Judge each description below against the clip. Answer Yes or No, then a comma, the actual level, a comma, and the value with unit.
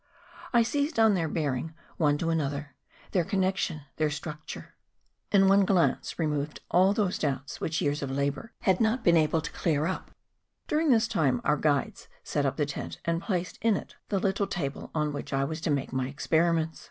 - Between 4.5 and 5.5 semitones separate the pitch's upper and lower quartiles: Yes, average, 4.9 semitones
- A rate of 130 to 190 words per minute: No, fast, 205 wpm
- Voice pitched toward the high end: No, medium, 165 Hz